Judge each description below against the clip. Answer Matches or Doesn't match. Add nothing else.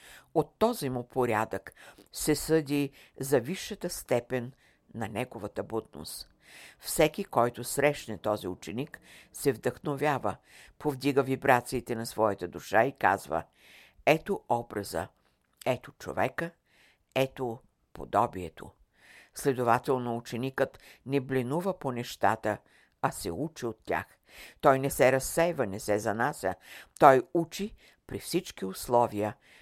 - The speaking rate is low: Matches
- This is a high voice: Doesn't match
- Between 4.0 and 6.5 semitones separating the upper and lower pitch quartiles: Matches